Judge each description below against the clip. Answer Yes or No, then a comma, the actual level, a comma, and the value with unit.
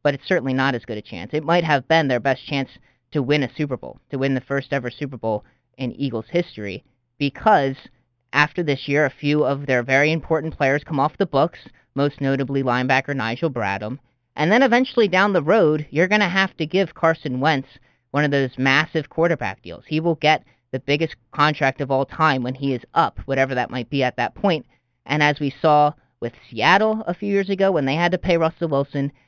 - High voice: No, medium, 140 Hz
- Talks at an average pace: No, fast, 220 wpm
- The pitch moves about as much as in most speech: Yes, average, 3.8 semitones